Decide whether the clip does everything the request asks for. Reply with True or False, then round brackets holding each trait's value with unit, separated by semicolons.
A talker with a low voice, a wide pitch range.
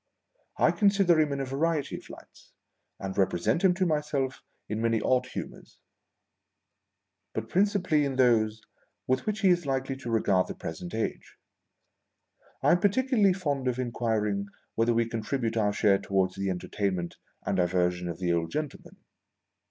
True (120 Hz; 7.4 semitones)